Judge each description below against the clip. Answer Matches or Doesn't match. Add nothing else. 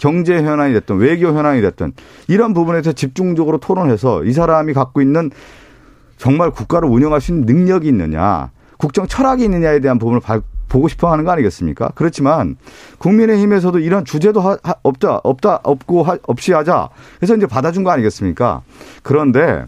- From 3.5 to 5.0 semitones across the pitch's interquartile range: Doesn't match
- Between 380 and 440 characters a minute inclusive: Matches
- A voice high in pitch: Doesn't match